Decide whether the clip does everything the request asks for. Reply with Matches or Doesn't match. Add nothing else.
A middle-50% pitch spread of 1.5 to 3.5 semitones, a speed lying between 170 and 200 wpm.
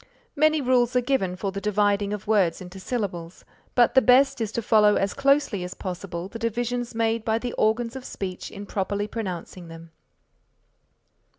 Doesn't match